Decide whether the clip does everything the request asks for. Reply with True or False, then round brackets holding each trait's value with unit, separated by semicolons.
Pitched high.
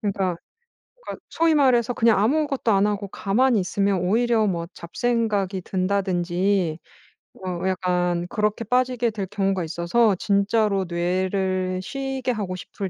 True (200 Hz)